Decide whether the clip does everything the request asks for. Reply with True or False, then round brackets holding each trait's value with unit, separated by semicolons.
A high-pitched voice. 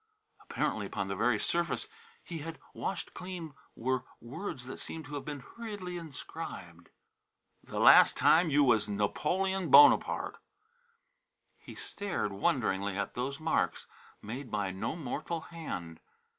False (140 Hz)